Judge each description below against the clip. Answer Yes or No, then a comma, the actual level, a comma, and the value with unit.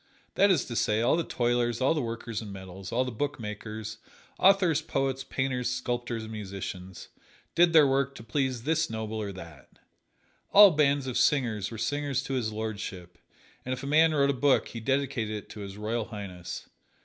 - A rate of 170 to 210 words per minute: Yes, average, 185 wpm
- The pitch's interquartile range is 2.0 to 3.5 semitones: No, average, 4.6 semitones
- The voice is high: No, low, 120 Hz